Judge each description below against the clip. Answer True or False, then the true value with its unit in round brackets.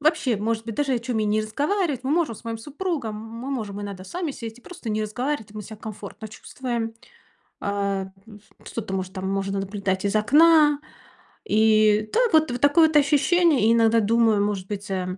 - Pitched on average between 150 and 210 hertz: False (225 Hz)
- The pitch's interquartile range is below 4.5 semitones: False (5.5 semitones)